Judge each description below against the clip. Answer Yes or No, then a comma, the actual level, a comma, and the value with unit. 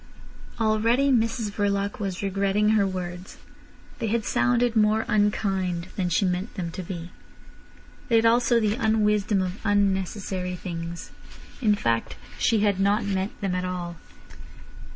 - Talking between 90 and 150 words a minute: Yes, average, 140 wpm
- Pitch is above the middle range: Yes, high, 200 Hz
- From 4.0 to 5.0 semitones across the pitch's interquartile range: No, average, 3.0 semitones